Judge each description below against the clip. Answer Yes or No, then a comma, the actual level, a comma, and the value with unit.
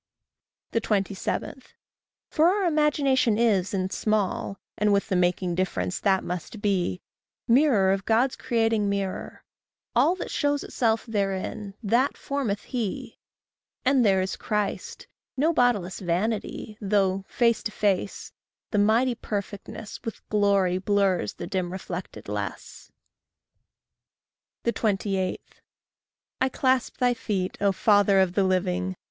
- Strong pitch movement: No, average, 3.7 semitones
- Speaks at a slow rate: Yes, slow, 120 wpm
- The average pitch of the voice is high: Yes, high, 205 Hz